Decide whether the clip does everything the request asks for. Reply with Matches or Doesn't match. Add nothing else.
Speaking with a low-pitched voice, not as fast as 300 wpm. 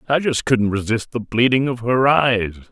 Matches